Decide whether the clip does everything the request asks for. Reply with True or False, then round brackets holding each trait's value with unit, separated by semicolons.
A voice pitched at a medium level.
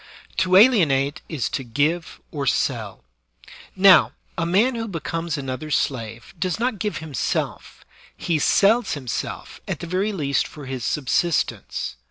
True (160 Hz)